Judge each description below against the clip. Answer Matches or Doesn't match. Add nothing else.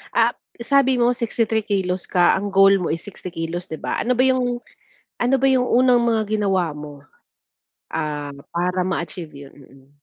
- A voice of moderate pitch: Doesn't match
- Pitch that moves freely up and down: Matches